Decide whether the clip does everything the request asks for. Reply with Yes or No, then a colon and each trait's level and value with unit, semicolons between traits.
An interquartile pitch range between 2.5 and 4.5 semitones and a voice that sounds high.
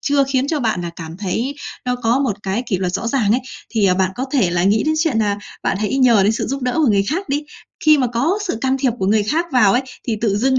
No: average, 5.1 semitones; high, 235 Hz